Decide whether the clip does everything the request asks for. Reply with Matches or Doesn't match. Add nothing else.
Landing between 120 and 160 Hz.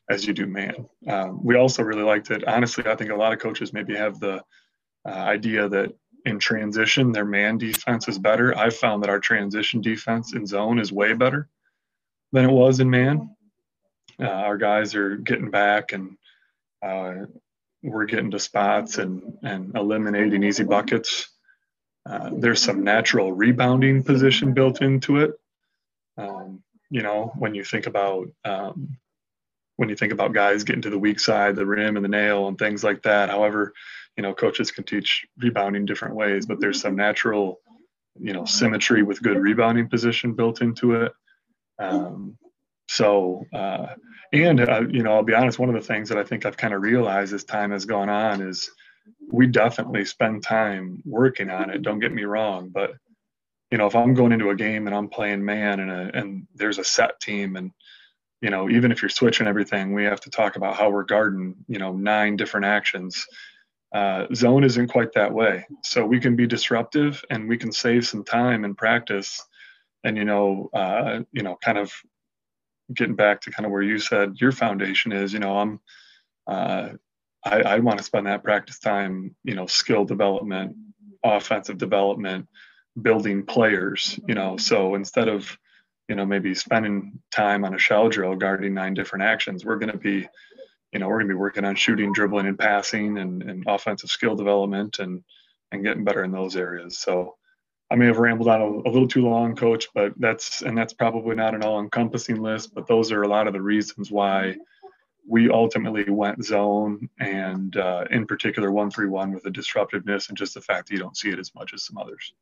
Doesn't match